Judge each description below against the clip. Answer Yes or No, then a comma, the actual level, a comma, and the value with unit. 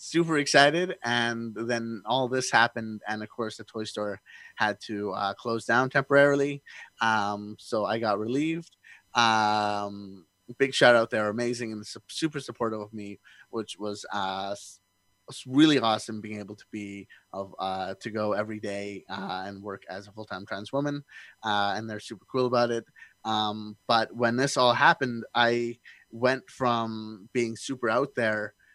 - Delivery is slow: No, average, 165 wpm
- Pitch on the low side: Yes, low, 110 Hz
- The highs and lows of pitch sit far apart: No, average, 2.9 semitones